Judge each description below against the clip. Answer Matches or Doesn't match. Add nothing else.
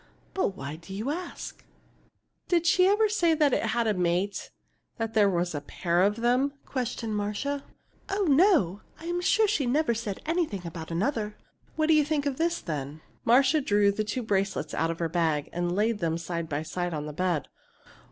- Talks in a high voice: Matches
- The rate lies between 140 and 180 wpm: Doesn't match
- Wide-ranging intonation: Matches